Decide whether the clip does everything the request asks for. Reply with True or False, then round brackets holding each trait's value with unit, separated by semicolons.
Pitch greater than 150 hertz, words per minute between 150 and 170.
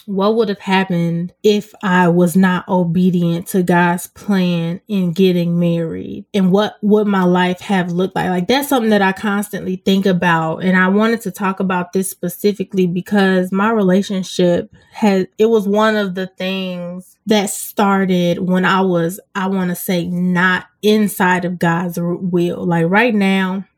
True (185 Hz; 165 wpm)